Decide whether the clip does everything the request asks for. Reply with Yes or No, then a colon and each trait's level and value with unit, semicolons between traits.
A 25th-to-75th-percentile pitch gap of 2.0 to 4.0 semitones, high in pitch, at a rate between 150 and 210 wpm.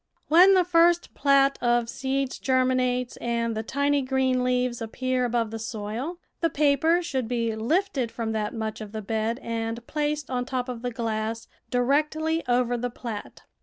Yes: average, 3.5 semitones; very high, 250 Hz; average, 165 wpm